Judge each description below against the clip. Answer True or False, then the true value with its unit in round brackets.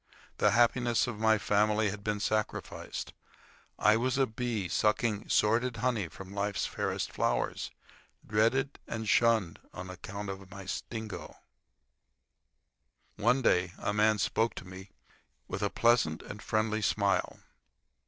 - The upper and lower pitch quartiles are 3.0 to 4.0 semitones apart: False (2.4 semitones)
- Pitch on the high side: False (105 Hz)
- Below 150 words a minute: True (135 wpm)